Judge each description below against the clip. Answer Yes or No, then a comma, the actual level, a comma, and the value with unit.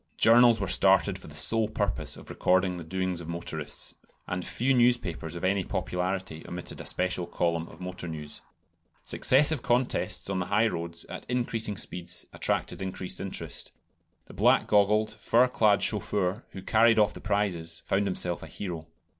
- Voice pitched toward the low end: Yes, very low, 95 Hz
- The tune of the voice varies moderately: Yes, average, 3.8 semitones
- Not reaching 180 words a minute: Yes, average, 165 wpm